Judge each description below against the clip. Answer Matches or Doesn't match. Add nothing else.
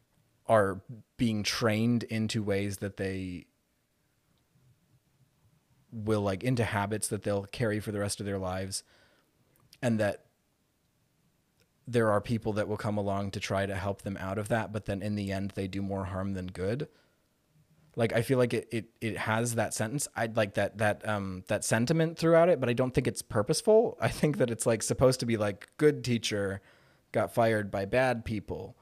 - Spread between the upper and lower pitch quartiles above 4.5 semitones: Doesn't match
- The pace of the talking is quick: Doesn't match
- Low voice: Matches